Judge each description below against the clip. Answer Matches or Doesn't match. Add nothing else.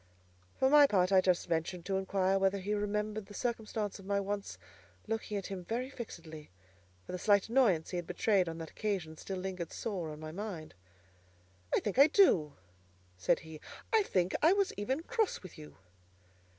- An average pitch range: Matches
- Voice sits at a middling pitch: Doesn't match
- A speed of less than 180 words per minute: Doesn't match